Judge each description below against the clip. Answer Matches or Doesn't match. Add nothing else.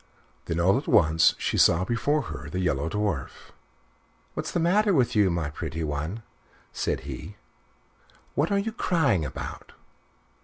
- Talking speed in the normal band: Matches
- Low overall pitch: Matches